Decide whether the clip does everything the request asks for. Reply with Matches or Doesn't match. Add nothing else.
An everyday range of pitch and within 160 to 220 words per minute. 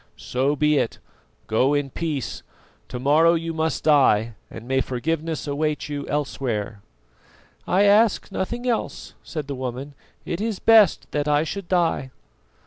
Doesn't match